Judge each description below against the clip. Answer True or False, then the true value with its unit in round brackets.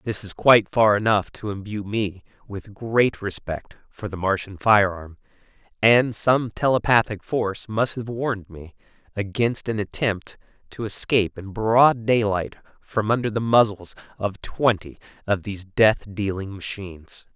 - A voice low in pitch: True (105 Hz)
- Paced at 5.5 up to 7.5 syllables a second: False (4.4 syllables/s)